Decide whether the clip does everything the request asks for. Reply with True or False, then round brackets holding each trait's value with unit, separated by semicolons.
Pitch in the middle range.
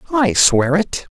True (175 Hz)